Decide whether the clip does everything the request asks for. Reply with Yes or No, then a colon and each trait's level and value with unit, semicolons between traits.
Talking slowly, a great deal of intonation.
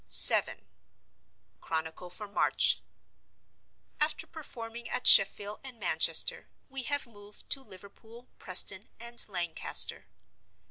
No: slow, 100 wpm; average, 4.4 semitones